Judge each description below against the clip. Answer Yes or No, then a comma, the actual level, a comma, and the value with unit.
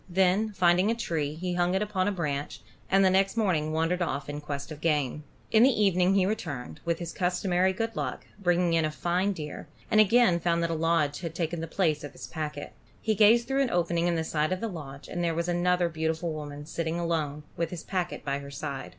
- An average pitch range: Yes, average, 3.3 semitones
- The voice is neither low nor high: Yes, medium, 170 Hz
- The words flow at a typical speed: No, fast, 235 wpm